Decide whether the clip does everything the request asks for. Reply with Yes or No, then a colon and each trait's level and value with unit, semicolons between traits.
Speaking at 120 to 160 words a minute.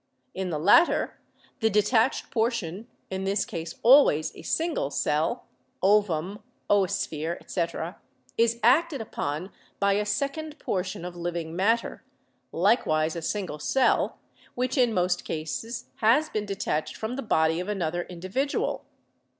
Yes: average, 140 wpm